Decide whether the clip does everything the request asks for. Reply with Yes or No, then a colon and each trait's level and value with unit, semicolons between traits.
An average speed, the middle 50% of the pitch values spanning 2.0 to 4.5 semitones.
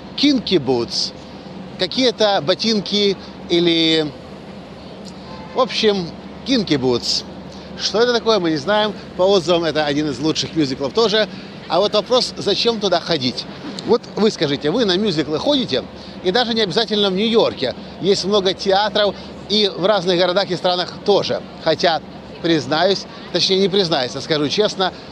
Yes: average, 145 wpm; average, 4.0 semitones